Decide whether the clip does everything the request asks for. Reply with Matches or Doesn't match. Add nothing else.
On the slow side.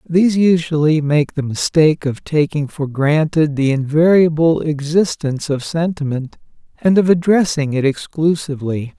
Matches